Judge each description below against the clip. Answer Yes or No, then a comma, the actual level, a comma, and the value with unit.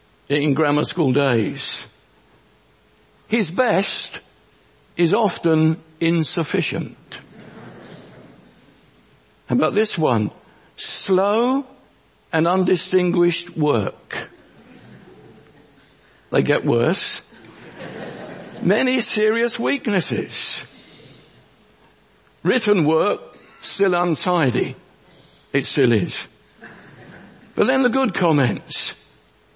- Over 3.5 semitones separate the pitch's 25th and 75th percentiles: Yes, average, 5.1 semitones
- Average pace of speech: No, slow, 70 wpm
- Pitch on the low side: No, medium, 180 Hz